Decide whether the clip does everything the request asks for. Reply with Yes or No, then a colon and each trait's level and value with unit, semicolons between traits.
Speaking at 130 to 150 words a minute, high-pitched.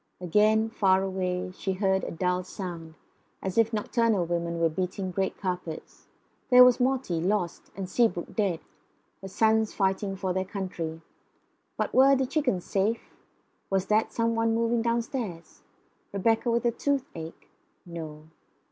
Yes: average, 145 wpm; high, 195 Hz